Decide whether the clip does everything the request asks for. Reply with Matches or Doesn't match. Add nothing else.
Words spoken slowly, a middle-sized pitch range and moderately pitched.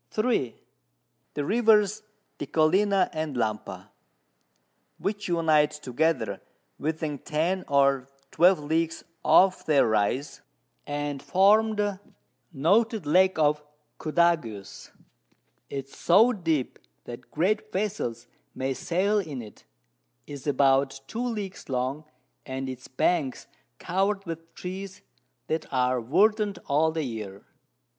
Doesn't match